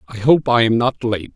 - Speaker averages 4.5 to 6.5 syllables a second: No, 4.2 syllables/s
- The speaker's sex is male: Yes, male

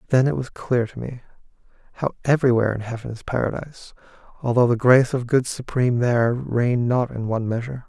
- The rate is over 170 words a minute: Yes, average, 185 wpm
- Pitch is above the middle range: No, low, 120 Hz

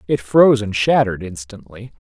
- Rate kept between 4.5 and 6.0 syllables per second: Yes, 5.6 syllables/s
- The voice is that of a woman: No, male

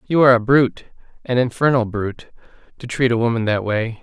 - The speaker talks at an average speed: Yes, average, 195 wpm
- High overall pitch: No, low, 120 Hz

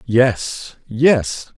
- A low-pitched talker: Yes, low, 120 Hz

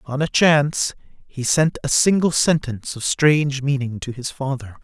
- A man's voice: Yes, male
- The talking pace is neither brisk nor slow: Yes, average, 175 wpm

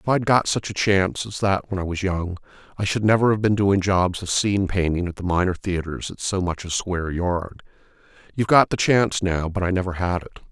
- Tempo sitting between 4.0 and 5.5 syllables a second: No, 5.7 syllables/s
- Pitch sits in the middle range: No, very low, 95 Hz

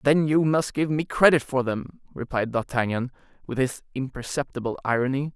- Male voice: Yes, male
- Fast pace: No, average, 155 wpm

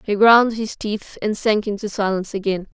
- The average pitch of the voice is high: Yes, high, 210 Hz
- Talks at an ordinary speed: Yes, average, 195 wpm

